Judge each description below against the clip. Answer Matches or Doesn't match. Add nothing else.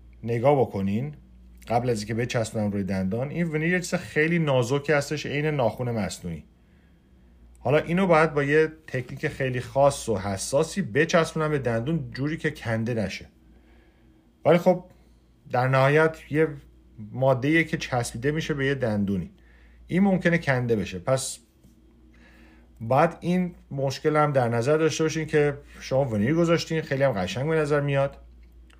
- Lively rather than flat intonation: Matches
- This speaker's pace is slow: Doesn't match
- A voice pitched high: Doesn't match